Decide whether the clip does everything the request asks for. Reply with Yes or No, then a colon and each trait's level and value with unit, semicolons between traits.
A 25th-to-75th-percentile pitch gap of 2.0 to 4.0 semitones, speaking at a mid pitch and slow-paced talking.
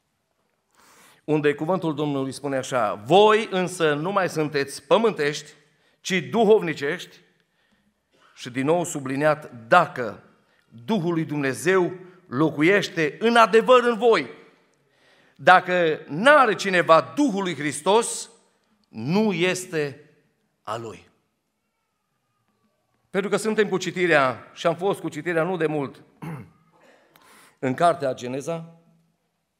No: average, 4.7 semitones; medium, 165 Hz; slow, 100 wpm